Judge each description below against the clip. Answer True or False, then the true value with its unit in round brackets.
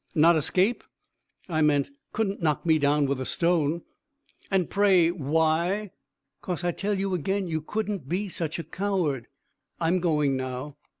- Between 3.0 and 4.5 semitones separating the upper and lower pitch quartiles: True (4.2 semitones)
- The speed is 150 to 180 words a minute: True (155 wpm)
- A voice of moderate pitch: True (170 Hz)